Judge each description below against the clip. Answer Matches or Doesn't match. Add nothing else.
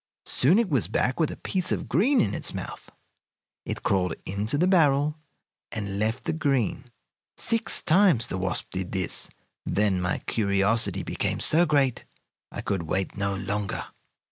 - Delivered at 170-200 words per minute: Doesn't match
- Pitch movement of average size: Doesn't match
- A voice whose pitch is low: Matches